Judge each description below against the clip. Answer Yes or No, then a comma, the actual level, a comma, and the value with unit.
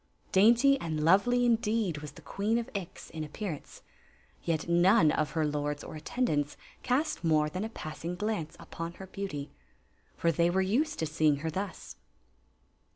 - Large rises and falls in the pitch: Yes, wide, 5.7 semitones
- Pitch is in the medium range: Yes, medium, 170 Hz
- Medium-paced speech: Yes, average, 160 wpm